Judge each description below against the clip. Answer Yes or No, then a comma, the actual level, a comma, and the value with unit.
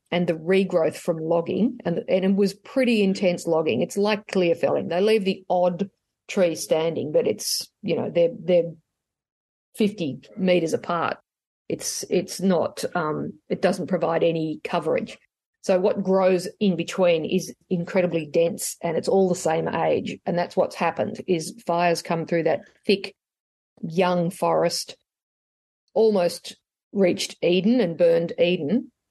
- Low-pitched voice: No, medium, 180 Hz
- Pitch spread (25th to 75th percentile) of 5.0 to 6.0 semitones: No, average, 2.8 semitones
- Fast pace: No, average, 150 wpm